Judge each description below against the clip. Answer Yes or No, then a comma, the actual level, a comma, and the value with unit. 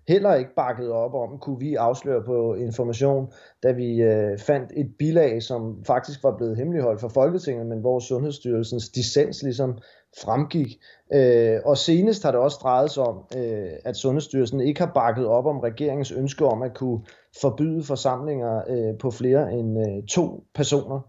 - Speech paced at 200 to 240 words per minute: No, average, 155 wpm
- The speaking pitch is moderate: No, low, 130 Hz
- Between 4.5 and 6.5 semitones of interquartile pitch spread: No, average, 3.5 semitones